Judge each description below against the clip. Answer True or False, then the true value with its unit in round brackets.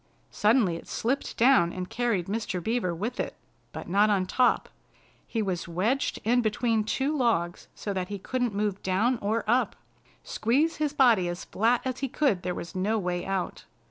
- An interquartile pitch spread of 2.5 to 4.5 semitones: False (4.9 semitones)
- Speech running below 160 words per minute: False (180 wpm)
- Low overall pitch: False (215 Hz)